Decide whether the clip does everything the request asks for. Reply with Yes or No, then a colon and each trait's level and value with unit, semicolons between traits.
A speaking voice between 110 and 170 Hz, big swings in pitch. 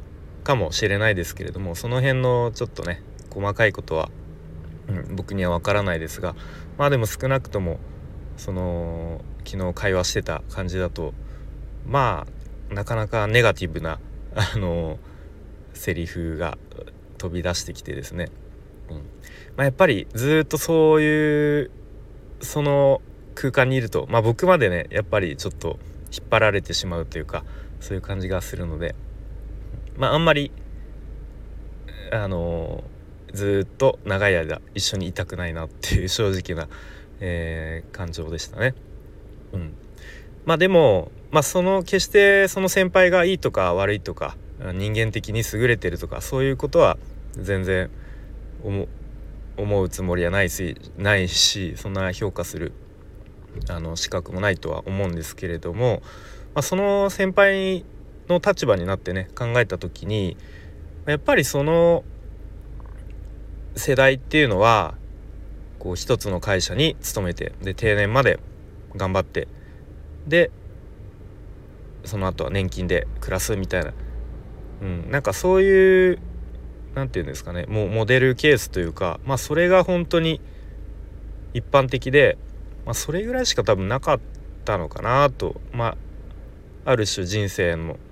No: very low, 95 Hz; wide, 6.4 semitones